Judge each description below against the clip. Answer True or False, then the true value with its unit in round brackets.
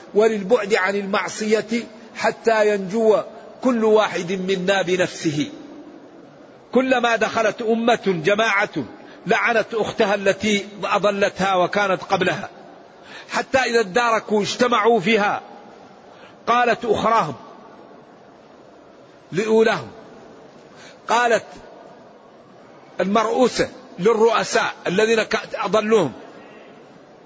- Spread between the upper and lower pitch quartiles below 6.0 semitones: True (2.6 semitones)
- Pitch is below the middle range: False (220 Hz)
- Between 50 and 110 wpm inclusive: True (70 wpm)